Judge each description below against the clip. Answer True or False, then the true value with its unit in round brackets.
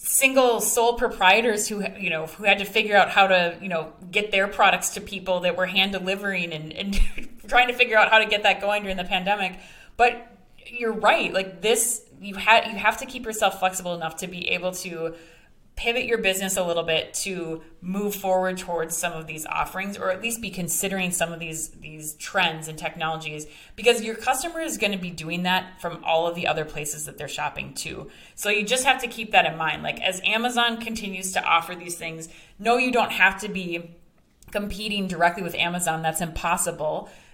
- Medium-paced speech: False (210 wpm)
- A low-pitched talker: False (190 Hz)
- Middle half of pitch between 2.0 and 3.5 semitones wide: False (4.0 semitones)